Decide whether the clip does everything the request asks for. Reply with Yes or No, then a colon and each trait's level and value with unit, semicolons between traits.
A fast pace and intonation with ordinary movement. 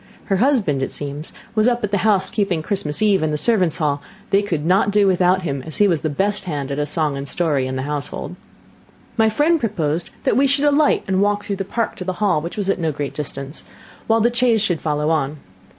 No: fast, 240 wpm; wide, 5.8 semitones